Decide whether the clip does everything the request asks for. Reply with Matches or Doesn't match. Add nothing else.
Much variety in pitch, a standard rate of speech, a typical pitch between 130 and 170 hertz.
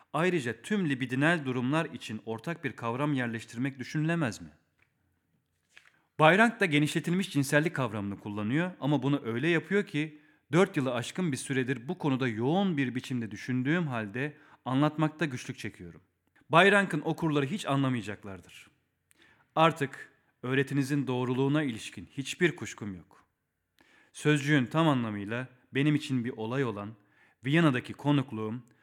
Doesn't match